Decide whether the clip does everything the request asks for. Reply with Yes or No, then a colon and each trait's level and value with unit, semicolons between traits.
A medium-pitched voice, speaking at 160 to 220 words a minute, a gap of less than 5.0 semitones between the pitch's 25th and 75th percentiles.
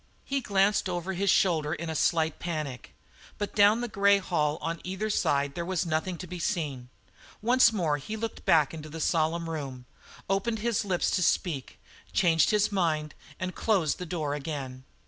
Yes: medium, 170 Hz; average, 180 wpm; average, 4.4 semitones